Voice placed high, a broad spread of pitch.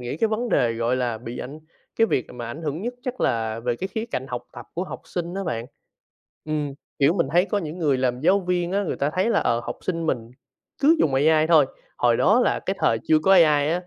No: medium, 155 Hz; wide, 6.9 semitones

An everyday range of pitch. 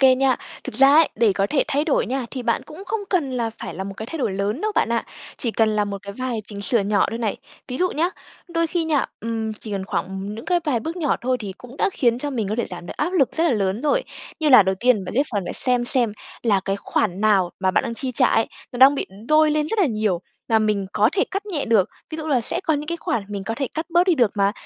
No: wide, 6.2 semitones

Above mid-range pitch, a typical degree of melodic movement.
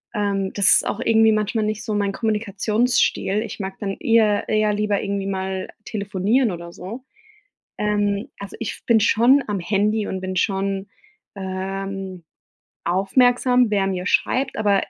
No: high, 205 Hz; narrow, 2.1 semitones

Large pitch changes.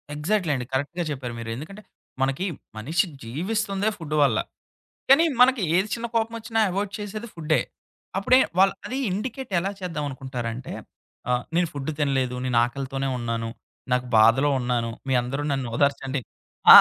Yes: wide, 7.7 semitones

